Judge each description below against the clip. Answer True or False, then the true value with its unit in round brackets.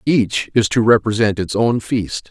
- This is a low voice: True (110 Hz)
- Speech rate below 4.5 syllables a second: True (4.2 syllables/s)